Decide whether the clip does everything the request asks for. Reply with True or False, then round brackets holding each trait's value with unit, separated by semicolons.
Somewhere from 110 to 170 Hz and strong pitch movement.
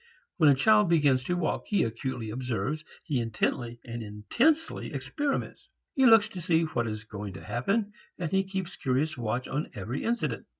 True (140 Hz; 8.5 semitones)